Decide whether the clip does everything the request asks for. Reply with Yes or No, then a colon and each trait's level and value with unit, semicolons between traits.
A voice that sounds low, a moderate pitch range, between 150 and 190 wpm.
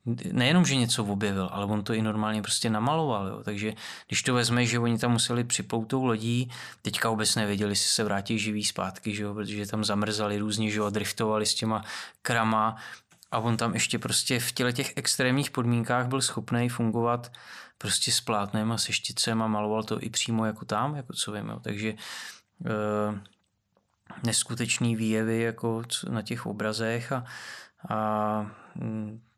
No: low, 110 Hz; narrow, 2.0 semitones; average, 165 wpm